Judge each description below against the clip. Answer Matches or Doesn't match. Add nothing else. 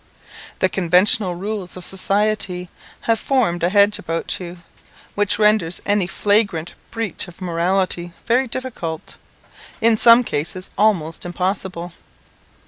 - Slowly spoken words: Matches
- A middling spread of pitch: Matches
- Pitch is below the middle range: Doesn't match